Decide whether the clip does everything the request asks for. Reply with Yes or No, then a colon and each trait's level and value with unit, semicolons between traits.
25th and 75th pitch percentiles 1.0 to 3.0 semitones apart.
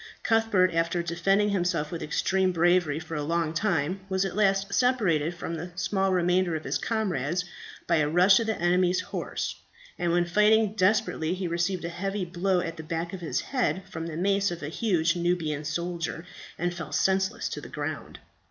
Yes: narrow, 2.6 semitones